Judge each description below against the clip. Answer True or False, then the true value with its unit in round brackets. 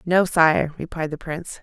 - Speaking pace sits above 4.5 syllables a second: True (4.7 syllables/s)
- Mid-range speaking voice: True (165 Hz)